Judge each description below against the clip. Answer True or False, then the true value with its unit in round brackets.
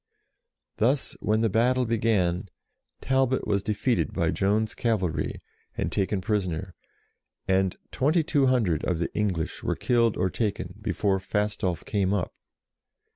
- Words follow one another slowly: True (125 wpm)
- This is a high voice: False (105 Hz)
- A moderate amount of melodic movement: True (3.8 semitones)